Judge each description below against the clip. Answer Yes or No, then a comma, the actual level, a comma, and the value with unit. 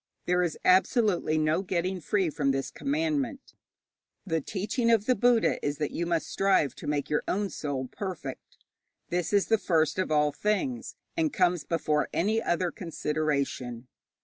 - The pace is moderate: Yes, average, 160 wpm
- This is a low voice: No, medium, 180 Hz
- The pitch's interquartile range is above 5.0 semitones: Yes, wide, 5.5 semitones